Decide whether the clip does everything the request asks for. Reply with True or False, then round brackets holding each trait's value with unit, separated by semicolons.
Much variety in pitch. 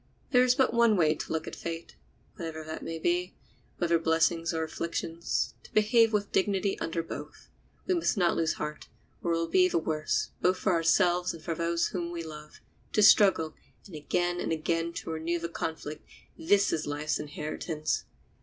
False (2.4 semitones)